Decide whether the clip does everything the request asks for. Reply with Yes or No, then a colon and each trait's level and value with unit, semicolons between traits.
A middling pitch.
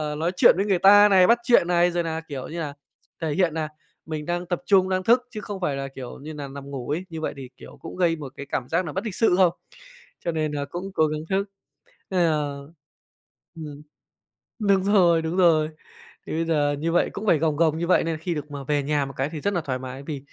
Yes: medium, 160 Hz